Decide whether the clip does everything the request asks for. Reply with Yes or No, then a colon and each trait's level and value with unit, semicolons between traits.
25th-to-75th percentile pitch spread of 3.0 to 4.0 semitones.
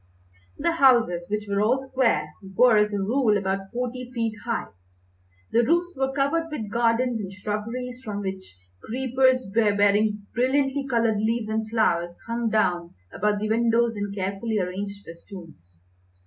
Yes: average, 3.7 semitones